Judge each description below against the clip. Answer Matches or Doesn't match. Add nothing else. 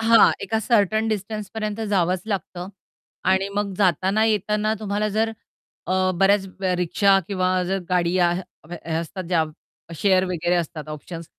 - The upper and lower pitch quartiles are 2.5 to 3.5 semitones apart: Matches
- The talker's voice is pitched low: Doesn't match